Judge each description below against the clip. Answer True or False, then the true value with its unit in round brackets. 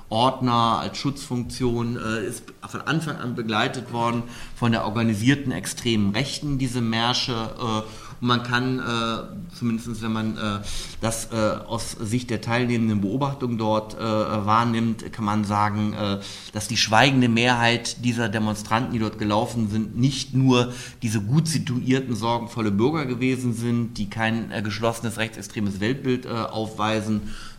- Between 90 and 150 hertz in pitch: True (115 Hz)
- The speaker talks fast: False (145 wpm)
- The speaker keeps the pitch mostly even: True (2.2 semitones)